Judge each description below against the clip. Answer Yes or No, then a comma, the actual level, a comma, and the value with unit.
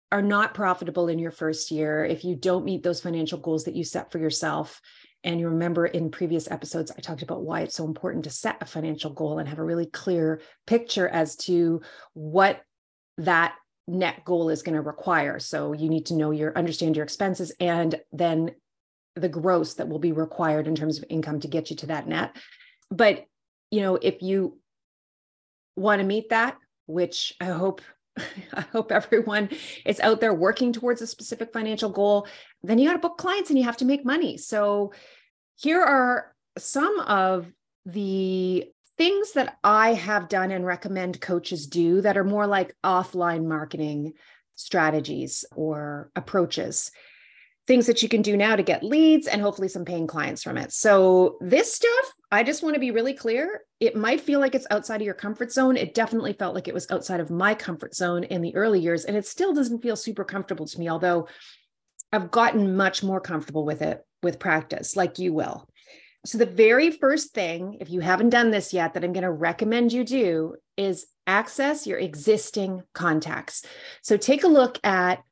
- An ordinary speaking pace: Yes, average, 190 wpm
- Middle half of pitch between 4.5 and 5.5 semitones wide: Yes, average, 5.1 semitones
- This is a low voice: No, medium, 185 Hz